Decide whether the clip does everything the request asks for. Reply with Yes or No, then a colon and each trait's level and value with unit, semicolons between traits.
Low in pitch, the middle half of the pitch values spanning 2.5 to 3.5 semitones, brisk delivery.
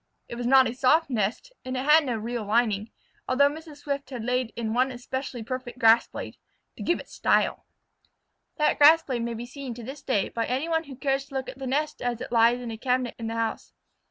No: very high, 255 Hz; average, 2.9 semitones; fast, 235 wpm